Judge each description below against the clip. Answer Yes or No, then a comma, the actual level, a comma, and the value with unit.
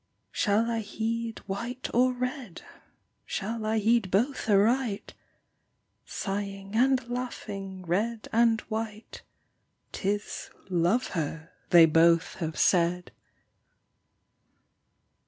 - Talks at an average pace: No, slow, 100 wpm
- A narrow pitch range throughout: No, average, 3.5 semitones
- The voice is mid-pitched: No, high, 215 Hz